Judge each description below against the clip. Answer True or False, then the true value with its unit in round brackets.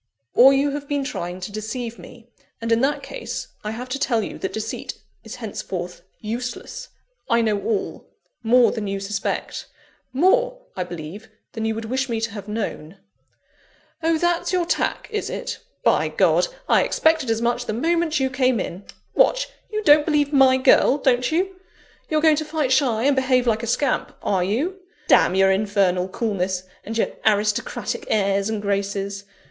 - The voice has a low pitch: False (235 Hz)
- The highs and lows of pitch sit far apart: True (5.8 semitones)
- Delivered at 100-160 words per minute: False (175 wpm)